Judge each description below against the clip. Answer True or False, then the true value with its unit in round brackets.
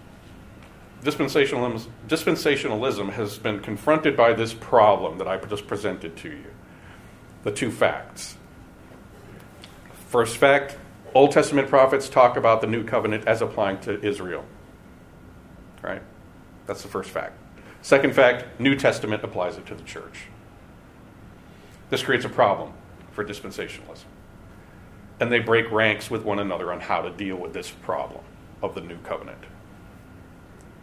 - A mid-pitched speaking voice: False (105 Hz)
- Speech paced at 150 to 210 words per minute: False (135 wpm)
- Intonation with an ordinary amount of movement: True (4.2 semitones)